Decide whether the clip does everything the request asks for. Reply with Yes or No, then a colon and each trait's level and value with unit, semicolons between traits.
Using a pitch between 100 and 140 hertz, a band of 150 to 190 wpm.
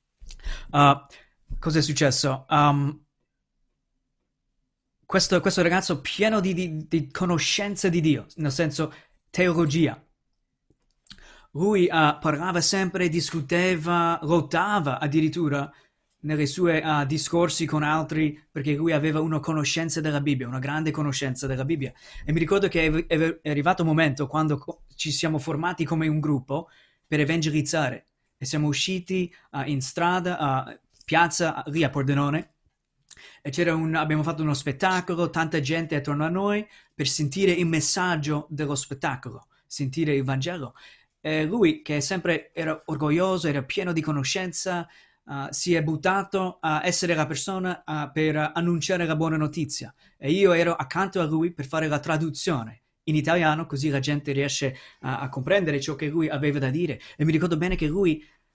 No: medium, 155 Hz; average, 155 wpm